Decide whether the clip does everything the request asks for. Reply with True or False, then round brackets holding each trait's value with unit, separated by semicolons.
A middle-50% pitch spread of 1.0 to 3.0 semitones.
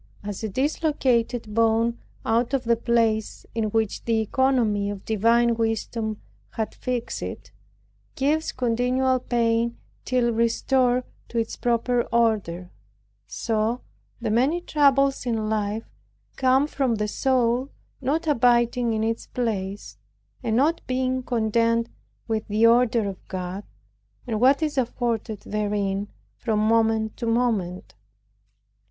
True (2.5 semitones)